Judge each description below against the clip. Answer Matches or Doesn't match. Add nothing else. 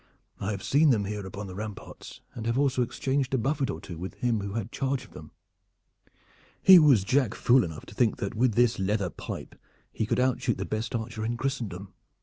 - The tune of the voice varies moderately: Matches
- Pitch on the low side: Matches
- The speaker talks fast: Matches